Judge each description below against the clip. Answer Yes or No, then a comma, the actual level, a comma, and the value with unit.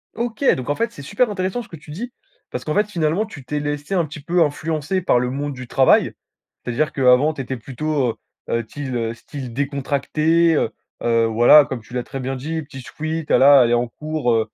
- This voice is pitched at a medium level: Yes, medium, 145 Hz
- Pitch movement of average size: Yes, average, 4.1 semitones